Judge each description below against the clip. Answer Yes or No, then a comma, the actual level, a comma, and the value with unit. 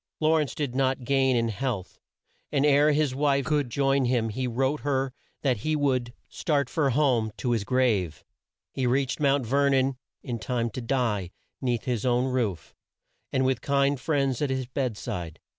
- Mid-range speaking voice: No, low, 130 Hz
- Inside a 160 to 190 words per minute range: Yes, average, 180 wpm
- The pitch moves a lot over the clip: No, narrow, 2.5 semitones